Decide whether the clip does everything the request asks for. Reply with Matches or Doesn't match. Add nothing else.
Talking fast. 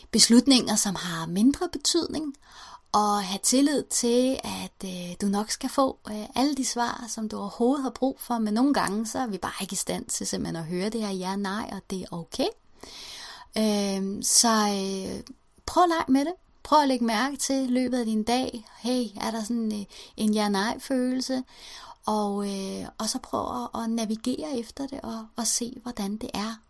Doesn't match